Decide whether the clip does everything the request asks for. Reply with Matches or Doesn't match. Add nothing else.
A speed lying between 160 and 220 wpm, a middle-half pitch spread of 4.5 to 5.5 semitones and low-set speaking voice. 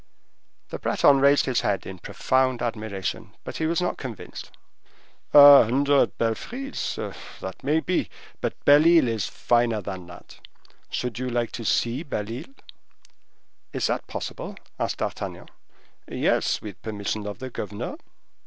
Doesn't match